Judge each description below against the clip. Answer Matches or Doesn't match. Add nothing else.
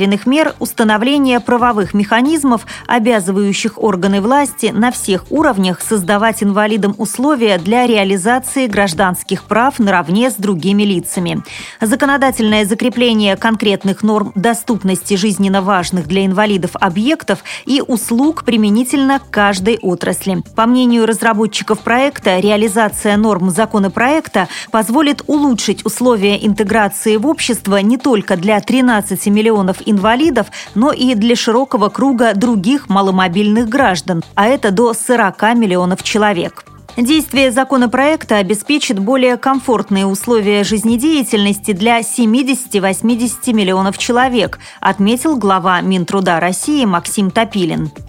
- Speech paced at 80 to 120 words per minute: Matches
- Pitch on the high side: Matches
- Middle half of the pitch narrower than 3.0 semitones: Doesn't match